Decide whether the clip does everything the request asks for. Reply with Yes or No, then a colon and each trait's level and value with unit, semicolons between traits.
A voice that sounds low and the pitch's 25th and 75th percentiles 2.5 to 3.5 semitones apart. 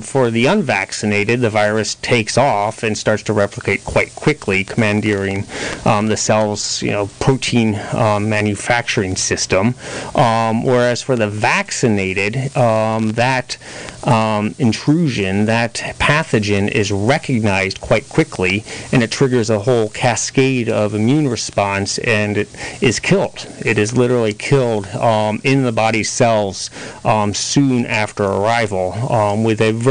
Yes: low, 110 Hz; average, 2.8 semitones